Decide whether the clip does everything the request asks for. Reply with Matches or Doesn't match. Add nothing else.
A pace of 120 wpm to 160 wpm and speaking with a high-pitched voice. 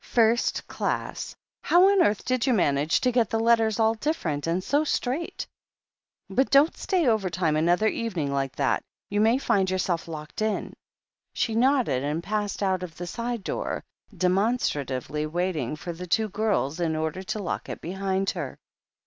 Doesn't match